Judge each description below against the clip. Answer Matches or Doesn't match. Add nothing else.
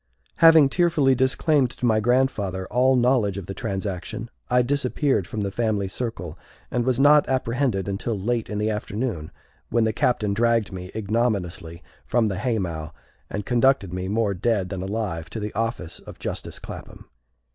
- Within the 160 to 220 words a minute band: Matches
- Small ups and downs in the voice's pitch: Doesn't match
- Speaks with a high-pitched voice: Doesn't match